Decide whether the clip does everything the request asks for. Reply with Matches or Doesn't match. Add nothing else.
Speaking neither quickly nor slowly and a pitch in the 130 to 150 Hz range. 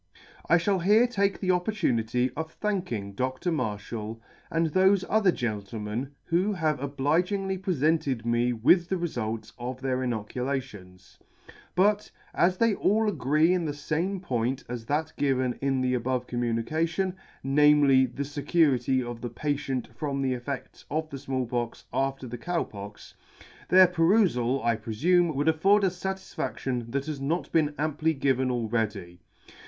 Matches